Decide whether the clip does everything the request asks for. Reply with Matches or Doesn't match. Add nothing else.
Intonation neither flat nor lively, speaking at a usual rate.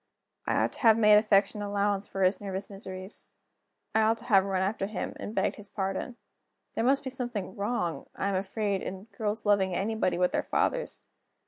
Doesn't match